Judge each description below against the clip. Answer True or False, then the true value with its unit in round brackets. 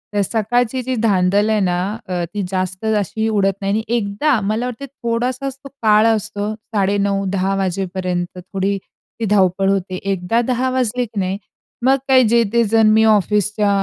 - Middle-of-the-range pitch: False (210 Hz)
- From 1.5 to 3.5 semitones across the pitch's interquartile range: True (3.1 semitones)